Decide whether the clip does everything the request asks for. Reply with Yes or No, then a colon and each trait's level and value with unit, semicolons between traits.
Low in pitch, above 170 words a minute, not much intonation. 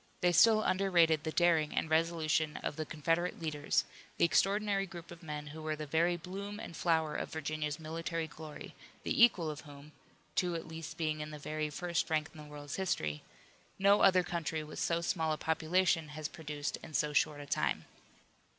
No: medium, 160 Hz; average, 190 wpm; narrow, 2.2 semitones